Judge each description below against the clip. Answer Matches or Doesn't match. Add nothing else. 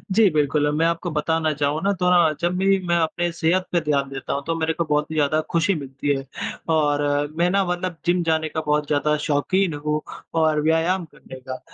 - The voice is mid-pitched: Matches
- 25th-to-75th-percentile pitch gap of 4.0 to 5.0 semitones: Doesn't match